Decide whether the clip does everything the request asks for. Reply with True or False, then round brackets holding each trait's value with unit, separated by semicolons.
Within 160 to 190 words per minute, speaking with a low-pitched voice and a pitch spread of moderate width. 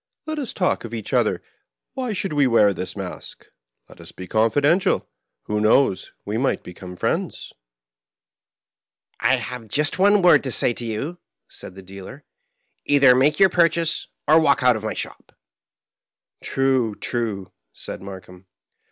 False (170 wpm; 125 Hz; 7.3 semitones)